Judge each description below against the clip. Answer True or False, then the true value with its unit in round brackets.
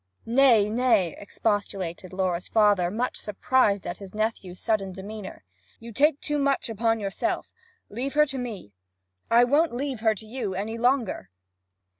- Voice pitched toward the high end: True (220 Hz)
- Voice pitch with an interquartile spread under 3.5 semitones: False (4.1 semitones)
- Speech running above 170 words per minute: False (150 wpm)